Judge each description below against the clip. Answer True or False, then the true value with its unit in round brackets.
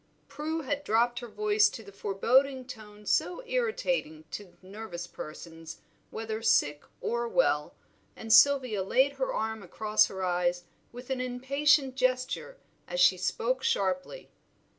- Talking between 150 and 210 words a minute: False (140 wpm)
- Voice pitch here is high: True (225 Hz)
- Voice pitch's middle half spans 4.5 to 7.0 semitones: True (5.4 semitones)